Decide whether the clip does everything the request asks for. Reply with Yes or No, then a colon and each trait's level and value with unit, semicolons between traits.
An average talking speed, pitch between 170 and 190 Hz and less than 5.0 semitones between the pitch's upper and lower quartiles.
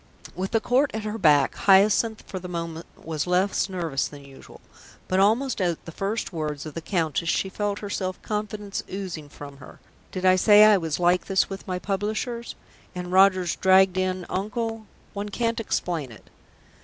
Yes: average, 180 wpm; medium, 185 Hz; average, 3.6 semitones